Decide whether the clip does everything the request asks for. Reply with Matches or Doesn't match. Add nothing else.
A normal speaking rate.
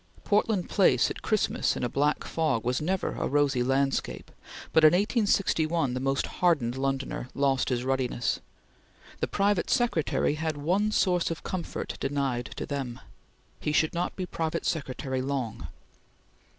Matches